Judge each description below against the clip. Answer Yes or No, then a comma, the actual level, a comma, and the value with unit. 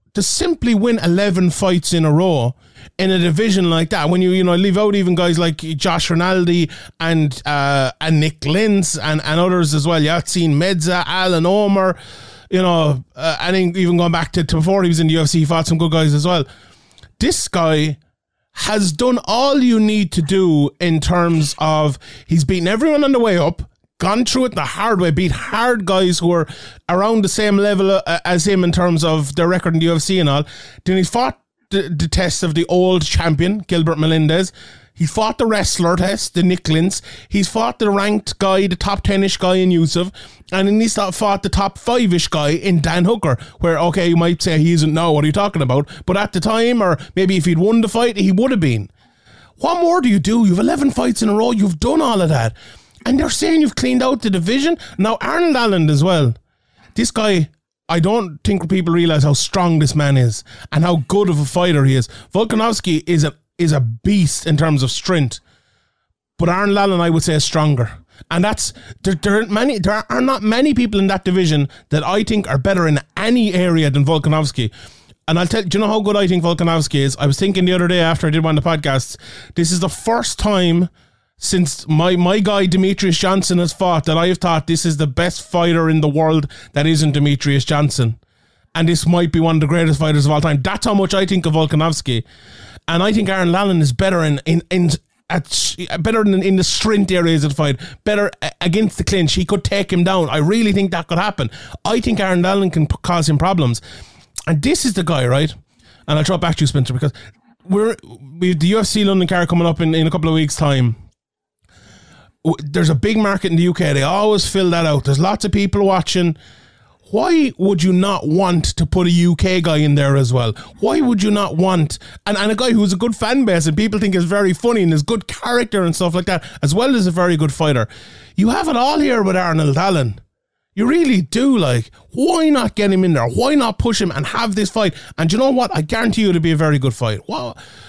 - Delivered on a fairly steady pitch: No, average, 4.3 semitones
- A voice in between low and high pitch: Yes, medium, 175 Hz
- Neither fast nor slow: No, fast, 225 wpm